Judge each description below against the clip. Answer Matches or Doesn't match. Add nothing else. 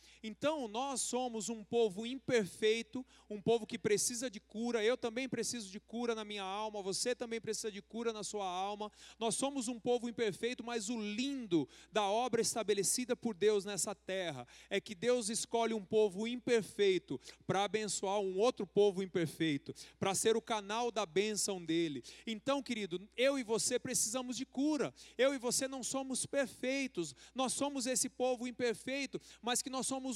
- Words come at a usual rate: Matches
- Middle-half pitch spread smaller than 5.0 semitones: Matches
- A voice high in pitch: Matches